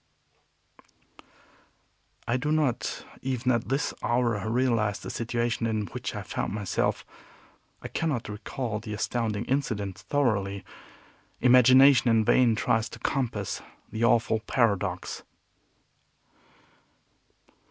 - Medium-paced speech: No, slow, 105 wpm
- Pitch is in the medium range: No, low, 115 Hz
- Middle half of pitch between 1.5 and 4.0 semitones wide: Yes, average, 3.1 semitones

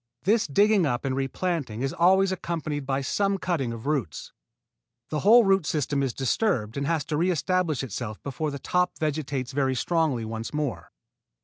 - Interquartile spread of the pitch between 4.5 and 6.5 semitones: Yes, average, 5.2 semitones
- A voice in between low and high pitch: Yes, medium, 150 Hz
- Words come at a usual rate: Yes, average, 175 wpm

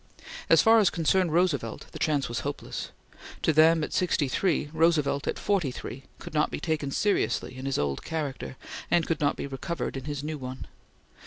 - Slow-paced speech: No, average, 190 wpm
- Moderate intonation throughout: Yes, average, 3.4 semitones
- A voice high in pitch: No, medium, 150 Hz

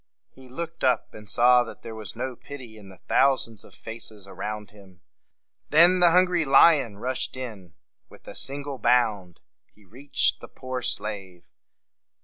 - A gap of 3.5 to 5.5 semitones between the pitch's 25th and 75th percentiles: Yes, average, 4.6 semitones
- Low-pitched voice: Yes, low, 120 Hz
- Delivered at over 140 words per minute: Yes, average, 160 wpm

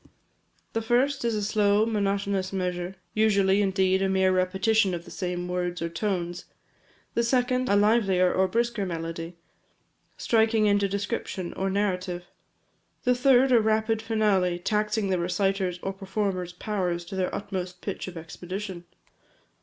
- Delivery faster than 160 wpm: No, average, 145 wpm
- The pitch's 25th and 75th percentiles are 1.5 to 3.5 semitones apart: Yes, average, 3.1 semitones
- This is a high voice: Yes, high, 195 Hz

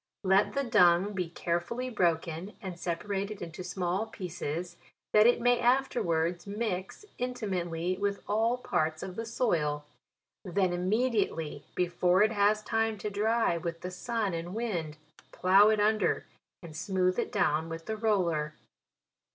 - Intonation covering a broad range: No, average, 4.1 semitones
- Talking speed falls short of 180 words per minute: Yes, average, 145 wpm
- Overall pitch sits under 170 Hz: No, high, 190 Hz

